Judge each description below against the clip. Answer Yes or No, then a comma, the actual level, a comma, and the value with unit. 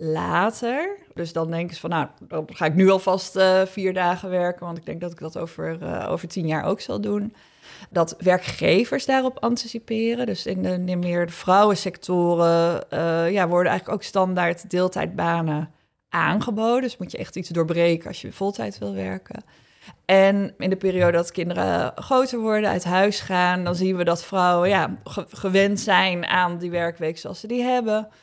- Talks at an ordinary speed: Yes, average, 185 wpm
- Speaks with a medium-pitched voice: Yes, medium, 180 Hz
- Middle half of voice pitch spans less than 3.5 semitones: Yes, average, 2.9 semitones